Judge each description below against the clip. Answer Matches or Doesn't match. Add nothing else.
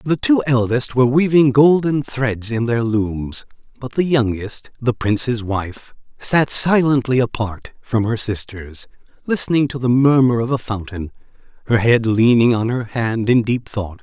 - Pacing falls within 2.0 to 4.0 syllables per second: Doesn't match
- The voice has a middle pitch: Doesn't match